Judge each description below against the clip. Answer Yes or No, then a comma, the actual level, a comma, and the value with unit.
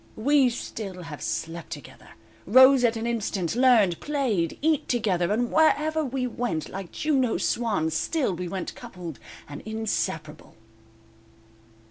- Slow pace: Yes, slow, 130 wpm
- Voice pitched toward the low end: No, high, 220 Hz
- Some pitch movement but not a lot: No, wide, 6.5 semitones